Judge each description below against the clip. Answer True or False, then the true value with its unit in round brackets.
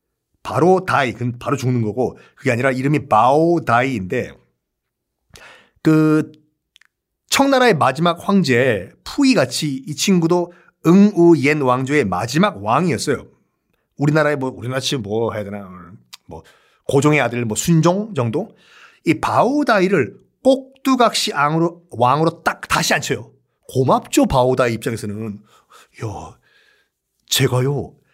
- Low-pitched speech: False (150 Hz)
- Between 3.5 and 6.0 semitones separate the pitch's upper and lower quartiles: True (5.6 semitones)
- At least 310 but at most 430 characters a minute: False (250 characters per minute)